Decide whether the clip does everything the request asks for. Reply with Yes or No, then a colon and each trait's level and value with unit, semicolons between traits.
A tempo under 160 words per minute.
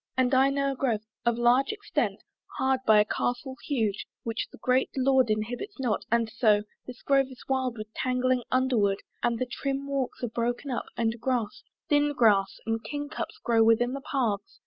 No: average, 190 wpm